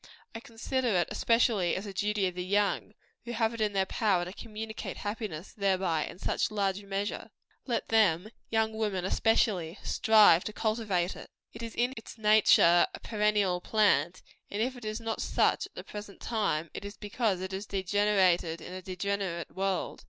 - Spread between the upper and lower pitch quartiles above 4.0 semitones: No, average, 2.9 semitones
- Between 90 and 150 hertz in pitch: No, high, 205 Hz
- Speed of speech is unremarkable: Yes, average, 185 wpm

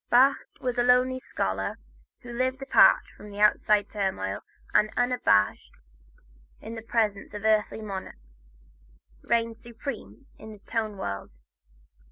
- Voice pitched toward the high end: Yes, high, 220 Hz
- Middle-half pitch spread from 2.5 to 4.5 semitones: Yes, average, 3.3 semitones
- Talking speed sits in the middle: No, slow, 125 wpm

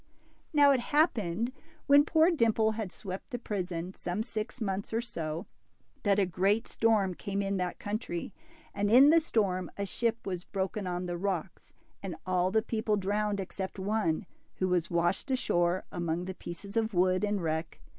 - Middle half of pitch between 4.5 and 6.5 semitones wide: No, average, 3.5 semitones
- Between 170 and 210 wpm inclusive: Yes, average, 175 wpm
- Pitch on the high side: Yes, high, 200 Hz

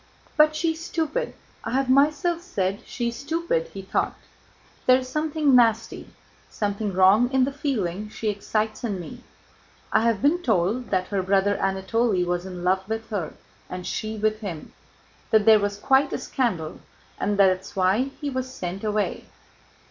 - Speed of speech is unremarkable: Yes, average, 170 wpm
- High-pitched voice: Yes, high, 220 Hz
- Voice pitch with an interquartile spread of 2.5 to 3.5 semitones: No, wide, 5.6 semitones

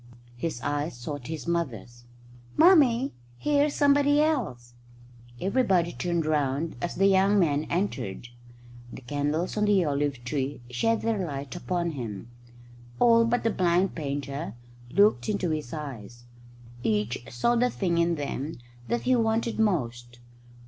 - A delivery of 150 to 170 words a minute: No, slow, 135 wpm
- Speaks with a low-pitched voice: No, medium, 165 Hz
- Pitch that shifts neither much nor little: No, wide, 7.5 semitones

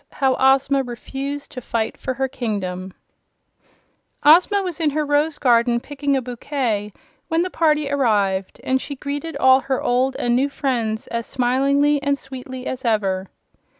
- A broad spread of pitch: No, average, 3.1 semitones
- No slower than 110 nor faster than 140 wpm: No, average, 155 wpm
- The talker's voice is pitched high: Yes, very high, 265 Hz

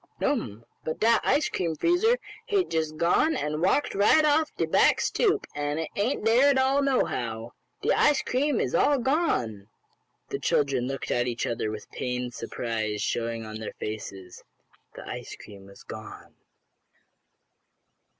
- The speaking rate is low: No, average, 155 wpm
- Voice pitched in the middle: Yes, medium, 155 Hz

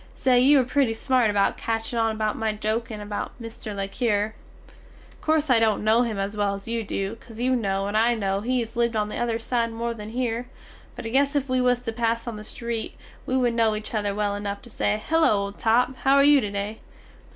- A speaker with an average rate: No, fast, 240 wpm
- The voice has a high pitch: Yes, high, 225 Hz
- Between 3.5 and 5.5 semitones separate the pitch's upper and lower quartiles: No, average, 2.7 semitones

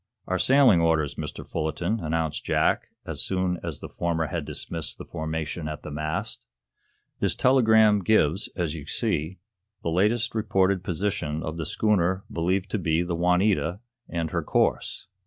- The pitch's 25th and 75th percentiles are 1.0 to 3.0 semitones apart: No, average, 3.6 semitones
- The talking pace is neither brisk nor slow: Yes, average, 155 wpm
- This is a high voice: No, very low, 85 Hz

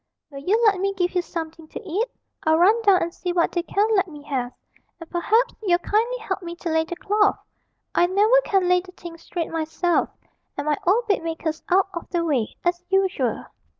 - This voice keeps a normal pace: No, fast, 210 wpm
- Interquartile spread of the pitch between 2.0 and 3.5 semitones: Yes, average, 3.1 semitones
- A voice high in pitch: Yes, very high, 355 Hz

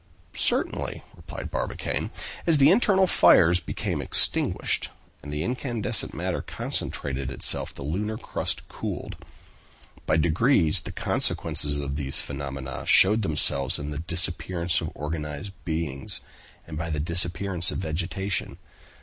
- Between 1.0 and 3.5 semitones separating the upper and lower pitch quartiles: No, average, 4.7 semitones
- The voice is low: Yes, very low, 85 Hz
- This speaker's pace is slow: Yes, slow, 125 wpm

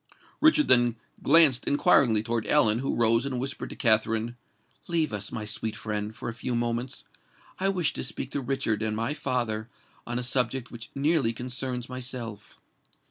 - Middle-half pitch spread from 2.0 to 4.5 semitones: Yes, average, 3.2 semitones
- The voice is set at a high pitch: No, low, 120 Hz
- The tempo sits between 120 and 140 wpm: No, average, 170 wpm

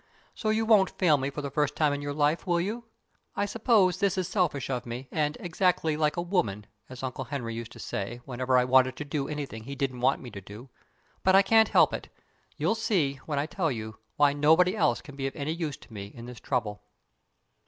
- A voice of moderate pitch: Yes, medium, 145 Hz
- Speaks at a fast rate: Yes, fast, 230 wpm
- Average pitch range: No, wide, 5.8 semitones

